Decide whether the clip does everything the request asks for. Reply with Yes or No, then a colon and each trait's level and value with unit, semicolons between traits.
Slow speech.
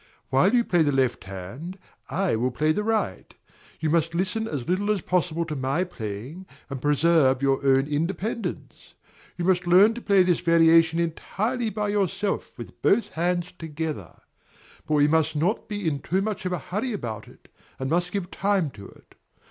No: average, 180 wpm